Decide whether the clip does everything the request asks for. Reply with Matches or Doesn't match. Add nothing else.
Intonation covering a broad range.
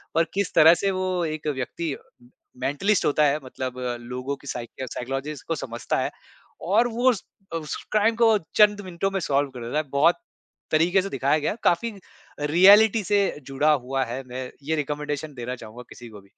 Matches